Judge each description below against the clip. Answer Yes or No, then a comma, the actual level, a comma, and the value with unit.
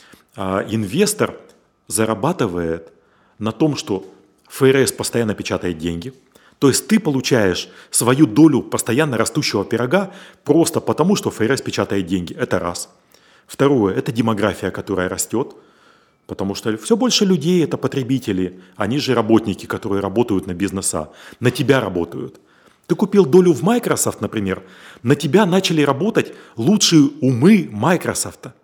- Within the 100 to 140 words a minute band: Yes, average, 130 wpm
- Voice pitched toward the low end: Yes, low, 115 Hz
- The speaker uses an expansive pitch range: Yes, wide, 7.7 semitones